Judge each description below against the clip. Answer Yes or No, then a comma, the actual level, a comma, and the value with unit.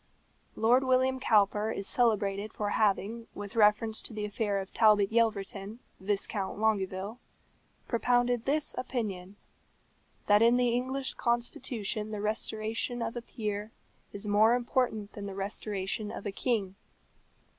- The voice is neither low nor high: No, high, 215 Hz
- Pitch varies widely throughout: No, average, 2.7 semitones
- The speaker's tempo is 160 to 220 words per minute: No, slow, 135 wpm